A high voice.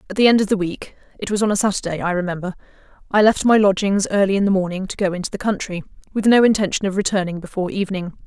Yes: high, 195 Hz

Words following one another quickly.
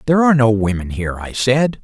Yes: fast, 230 wpm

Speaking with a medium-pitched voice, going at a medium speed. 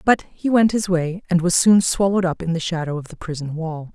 No: medium, 175 Hz; fast, 260 wpm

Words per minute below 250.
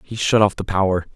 No: fast, 260 wpm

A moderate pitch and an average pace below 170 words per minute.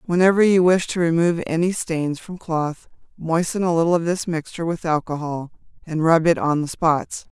No: medium, 165 Hz; average, 185 wpm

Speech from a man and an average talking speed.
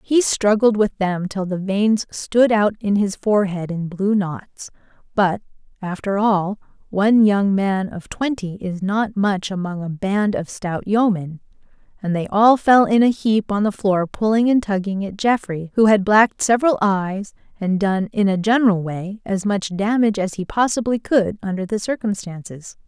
No: female; average, 180 wpm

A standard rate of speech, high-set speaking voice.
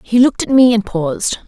No: fast, 245 wpm; high, 230 Hz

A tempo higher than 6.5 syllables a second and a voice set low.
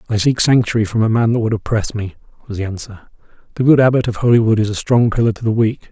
Yes: 6.8 syllables/s; low, 110 Hz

